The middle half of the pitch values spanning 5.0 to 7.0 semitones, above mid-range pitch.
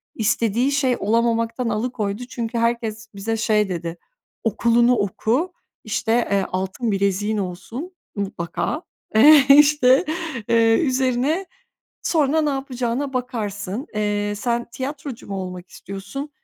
No: average, 4.1 semitones; high, 230 Hz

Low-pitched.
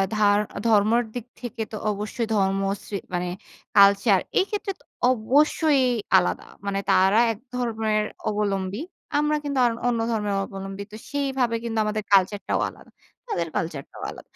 No: high, 215 Hz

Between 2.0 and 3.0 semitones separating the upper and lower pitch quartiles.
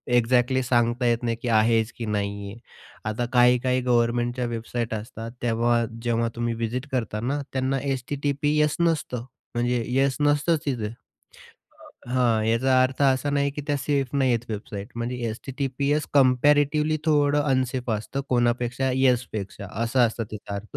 Yes: average, 2.7 semitones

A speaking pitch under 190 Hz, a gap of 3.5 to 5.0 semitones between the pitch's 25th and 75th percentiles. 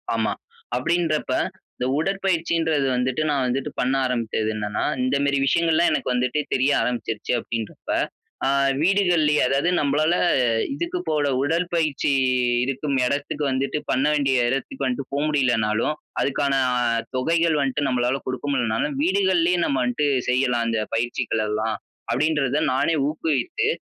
Yes: medium, 140 Hz; average, 4.0 semitones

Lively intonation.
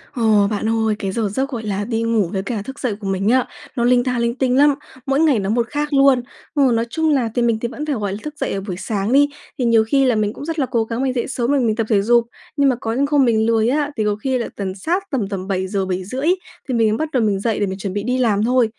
No: average, 4.1 semitones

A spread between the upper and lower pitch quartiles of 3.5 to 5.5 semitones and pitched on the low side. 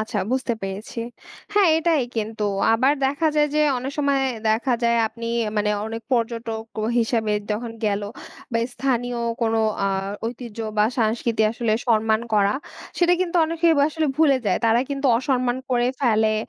No: average, 3.8 semitones; high, 235 Hz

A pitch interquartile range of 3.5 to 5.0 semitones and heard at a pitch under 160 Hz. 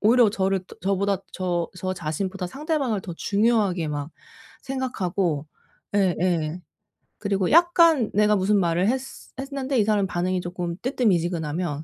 No: average, 4.6 semitones; high, 195 Hz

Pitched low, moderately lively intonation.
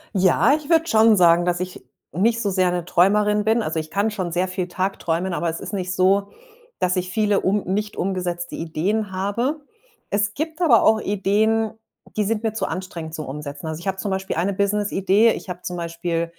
No: high, 190 Hz; average, 3.1 semitones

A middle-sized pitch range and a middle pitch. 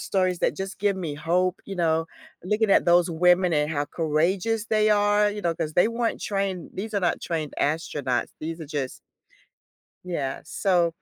Yes: average, 3.7 semitones; medium, 180 Hz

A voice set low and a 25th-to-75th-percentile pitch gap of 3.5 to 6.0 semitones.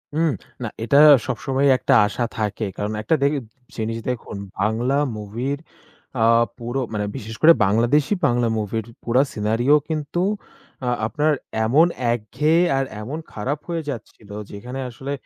Yes: low, 120 Hz; average, 4.4 semitones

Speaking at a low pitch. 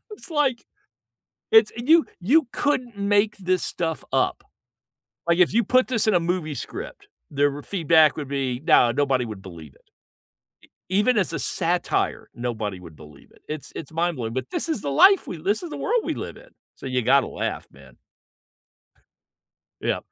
No: medium, 165 Hz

